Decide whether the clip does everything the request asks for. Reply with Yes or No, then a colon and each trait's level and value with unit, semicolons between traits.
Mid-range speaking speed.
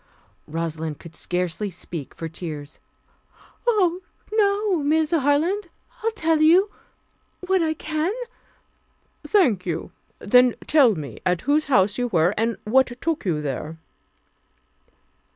No: slow, 125 wpm